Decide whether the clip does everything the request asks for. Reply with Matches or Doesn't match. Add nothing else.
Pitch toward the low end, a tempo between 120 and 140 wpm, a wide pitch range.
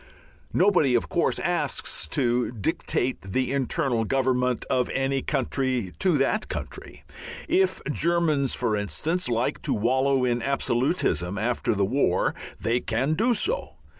Doesn't match